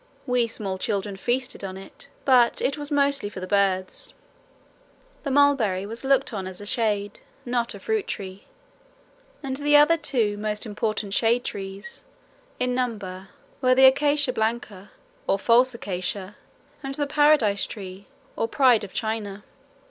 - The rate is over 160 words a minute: No, average, 150 wpm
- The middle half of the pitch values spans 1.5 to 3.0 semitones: No, average, 5.0 semitones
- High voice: Yes, high, 225 Hz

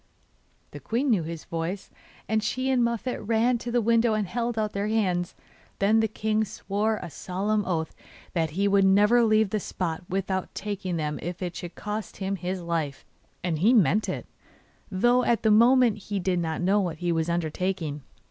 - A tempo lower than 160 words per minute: No, average, 190 wpm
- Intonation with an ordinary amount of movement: Yes, average, 3.9 semitones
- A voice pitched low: No, high, 200 Hz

